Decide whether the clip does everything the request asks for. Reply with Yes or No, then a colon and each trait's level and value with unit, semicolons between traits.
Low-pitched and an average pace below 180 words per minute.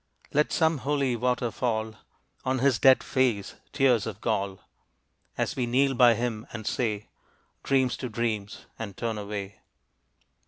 Yes: low, 120 Hz; average, 145 wpm